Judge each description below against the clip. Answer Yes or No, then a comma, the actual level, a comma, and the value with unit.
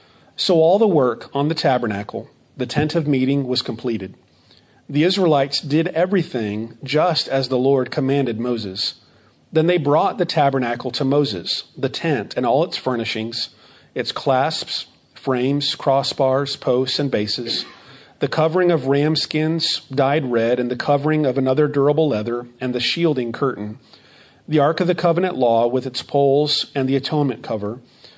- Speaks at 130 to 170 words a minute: Yes, average, 160 wpm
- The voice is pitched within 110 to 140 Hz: Yes, low, 135 Hz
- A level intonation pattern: No, average, 3.5 semitones